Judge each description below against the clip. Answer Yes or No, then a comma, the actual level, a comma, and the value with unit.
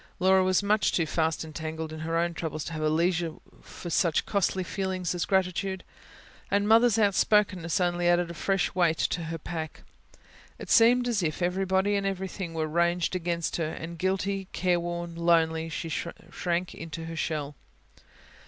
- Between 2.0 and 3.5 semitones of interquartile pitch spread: Yes, narrow, 2.6 semitones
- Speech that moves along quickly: No, average, 165 wpm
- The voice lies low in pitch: No, medium, 175 Hz